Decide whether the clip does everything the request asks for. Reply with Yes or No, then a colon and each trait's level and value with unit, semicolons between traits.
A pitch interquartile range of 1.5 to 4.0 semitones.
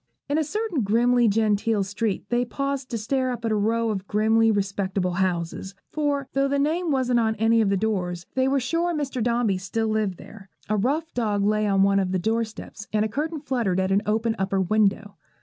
No: average, 4.4 semitones